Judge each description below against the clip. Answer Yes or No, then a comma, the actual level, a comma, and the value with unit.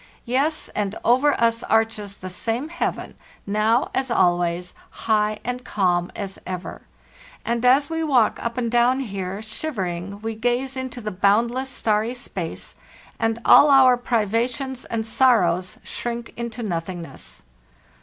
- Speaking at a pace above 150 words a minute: No, slow, 135 wpm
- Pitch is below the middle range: No, high, 230 Hz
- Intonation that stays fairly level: No, average, 3.9 semitones